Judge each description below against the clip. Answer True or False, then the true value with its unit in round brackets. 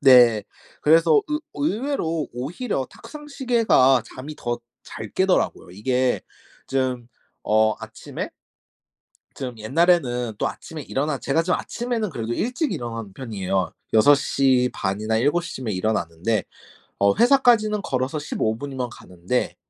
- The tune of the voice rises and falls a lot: True (7.2 semitones)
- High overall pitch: False (130 Hz)